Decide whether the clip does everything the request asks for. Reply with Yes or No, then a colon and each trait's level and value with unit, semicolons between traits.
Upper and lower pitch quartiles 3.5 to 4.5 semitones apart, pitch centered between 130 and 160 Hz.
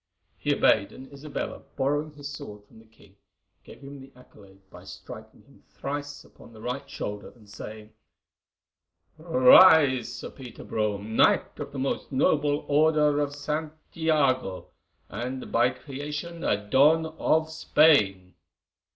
No: average, 5.2 semitones; medium, 140 Hz